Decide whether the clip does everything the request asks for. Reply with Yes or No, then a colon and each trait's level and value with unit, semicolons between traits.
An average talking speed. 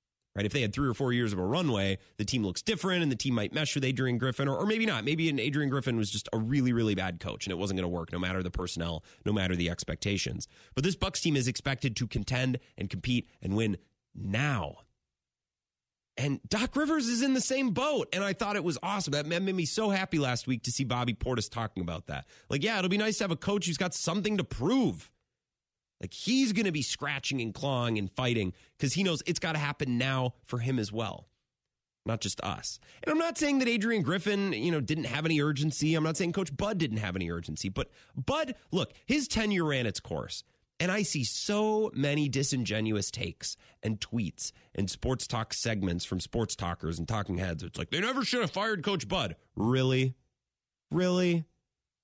No: fast, 220 wpm